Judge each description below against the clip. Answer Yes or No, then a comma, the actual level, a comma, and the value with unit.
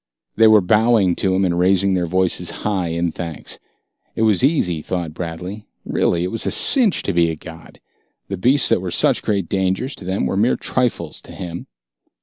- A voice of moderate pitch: No, very low, 95 Hz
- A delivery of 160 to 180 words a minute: No, average, 195 wpm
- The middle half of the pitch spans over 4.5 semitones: No, average, 3.5 semitones